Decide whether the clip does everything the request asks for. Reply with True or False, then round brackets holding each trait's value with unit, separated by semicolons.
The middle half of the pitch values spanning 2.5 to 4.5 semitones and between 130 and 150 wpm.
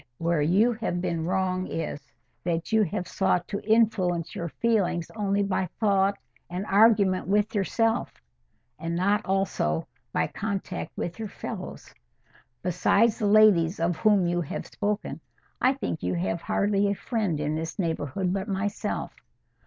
True (3.6 semitones; 145 wpm)